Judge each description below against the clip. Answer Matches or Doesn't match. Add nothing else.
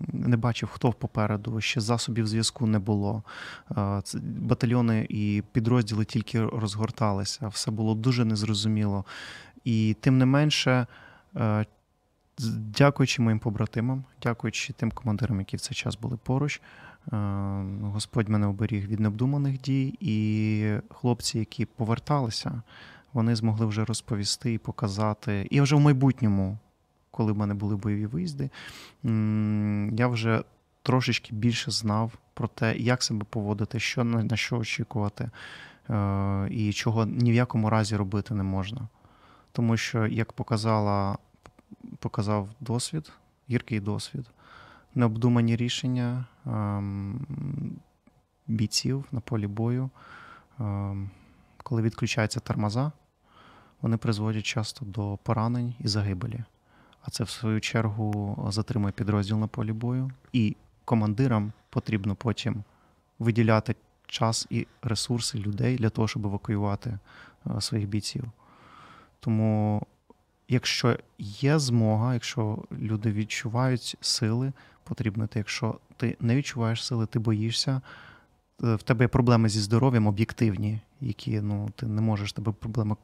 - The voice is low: Matches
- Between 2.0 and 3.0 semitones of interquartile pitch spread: Matches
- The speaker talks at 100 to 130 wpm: Matches